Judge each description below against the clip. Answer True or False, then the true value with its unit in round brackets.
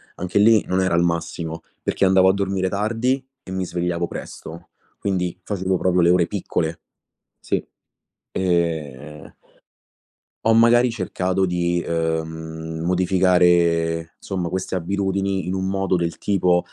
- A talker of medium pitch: False (90 Hz)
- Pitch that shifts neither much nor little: False (2.2 semitones)